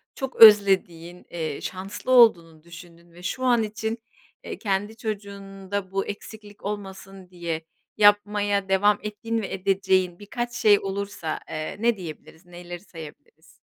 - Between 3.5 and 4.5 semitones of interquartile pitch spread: No, average, 2.9 semitones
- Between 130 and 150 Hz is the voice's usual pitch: No, high, 195 Hz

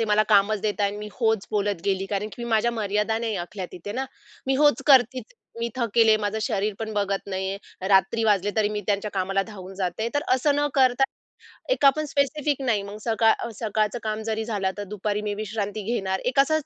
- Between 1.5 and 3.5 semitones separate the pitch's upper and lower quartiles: Yes, average, 2.7 semitones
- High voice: Yes, high, 215 Hz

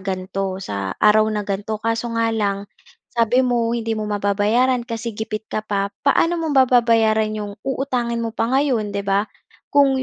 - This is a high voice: Yes, high, 225 Hz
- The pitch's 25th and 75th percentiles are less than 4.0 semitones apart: Yes, average, 2.8 semitones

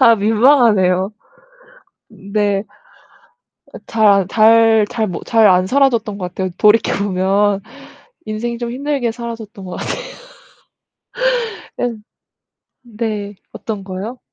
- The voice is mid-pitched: No, high, 215 Hz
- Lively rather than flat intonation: No, average, 2.9 semitones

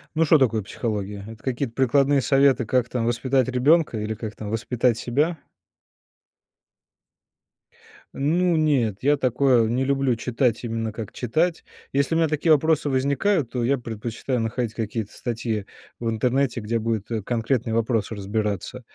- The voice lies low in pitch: Yes, low, 120 Hz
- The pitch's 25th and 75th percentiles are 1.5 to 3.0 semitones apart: No, average, 3.7 semitones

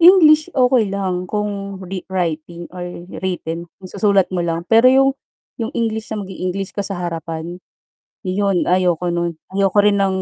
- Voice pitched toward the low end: No, high, 190 Hz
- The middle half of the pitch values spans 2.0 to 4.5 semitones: Yes, average, 3.0 semitones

